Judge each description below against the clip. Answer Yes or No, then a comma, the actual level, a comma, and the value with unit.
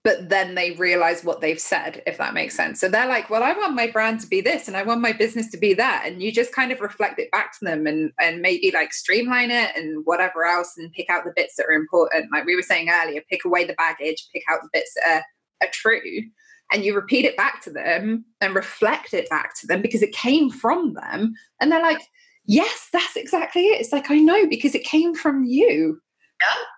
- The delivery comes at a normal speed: No, fast, 240 wpm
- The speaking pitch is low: No, high, 225 Hz